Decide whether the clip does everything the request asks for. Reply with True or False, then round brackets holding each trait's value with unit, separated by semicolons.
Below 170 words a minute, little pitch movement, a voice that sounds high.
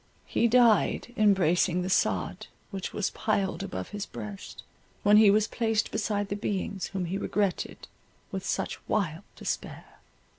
True (145 wpm; 1.9 semitones; 205 Hz)